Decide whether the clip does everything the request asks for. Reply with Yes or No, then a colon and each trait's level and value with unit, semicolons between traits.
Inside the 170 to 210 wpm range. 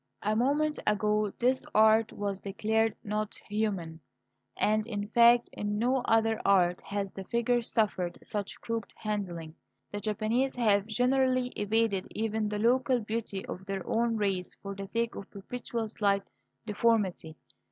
No: average, 145 wpm